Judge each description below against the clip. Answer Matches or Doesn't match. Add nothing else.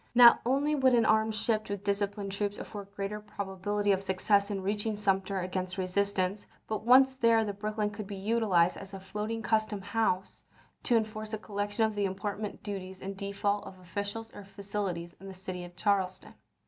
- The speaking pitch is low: Doesn't match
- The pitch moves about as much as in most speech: Doesn't match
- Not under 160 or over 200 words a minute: Matches